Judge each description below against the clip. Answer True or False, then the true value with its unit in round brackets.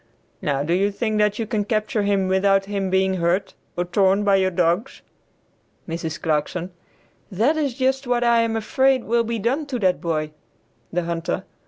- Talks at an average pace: True (180 wpm)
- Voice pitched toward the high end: True (200 Hz)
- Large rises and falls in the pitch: False (4.6 semitones)